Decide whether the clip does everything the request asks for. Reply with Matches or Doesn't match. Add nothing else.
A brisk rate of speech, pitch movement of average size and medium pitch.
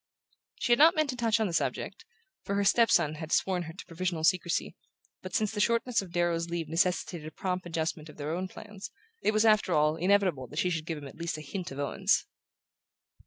Matches